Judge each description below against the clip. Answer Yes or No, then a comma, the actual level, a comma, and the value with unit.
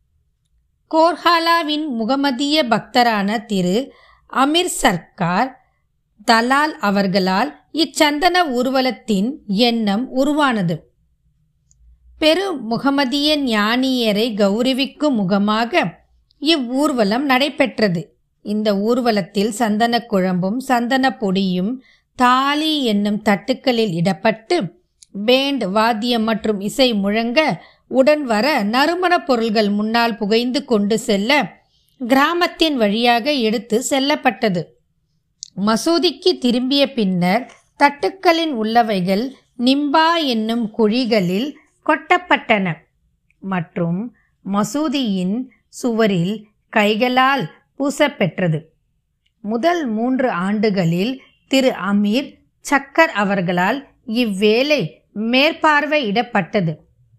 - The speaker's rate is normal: No, slow, 70 wpm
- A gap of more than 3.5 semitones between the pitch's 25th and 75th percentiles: Yes, average, 5.2 semitones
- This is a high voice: Yes, high, 235 Hz